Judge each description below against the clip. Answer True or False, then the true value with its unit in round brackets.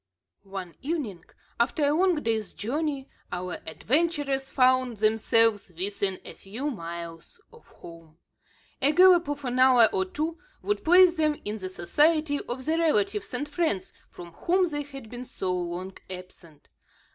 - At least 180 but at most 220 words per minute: False (150 wpm)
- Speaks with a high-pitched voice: True (250 Hz)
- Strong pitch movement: True (7.9 semitones)